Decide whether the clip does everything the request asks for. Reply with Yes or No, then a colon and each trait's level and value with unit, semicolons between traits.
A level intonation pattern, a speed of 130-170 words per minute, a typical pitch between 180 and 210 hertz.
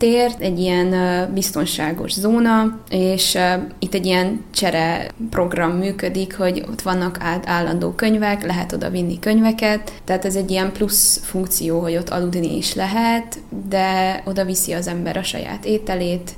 Yes: narrow, 2.3 semitones; average, 150 wpm; medium, 185 Hz